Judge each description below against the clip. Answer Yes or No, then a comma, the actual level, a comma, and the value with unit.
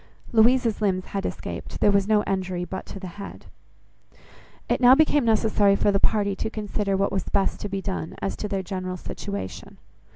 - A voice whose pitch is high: Yes, high, 200 Hz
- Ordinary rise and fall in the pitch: No, narrow, 2.2 semitones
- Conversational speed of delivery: Yes, average, 190 wpm